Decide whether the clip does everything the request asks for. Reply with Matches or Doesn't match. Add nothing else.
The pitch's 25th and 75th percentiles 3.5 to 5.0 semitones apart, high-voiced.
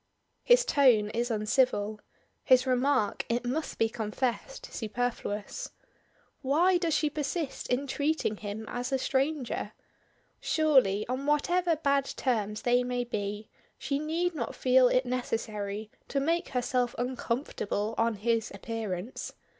Matches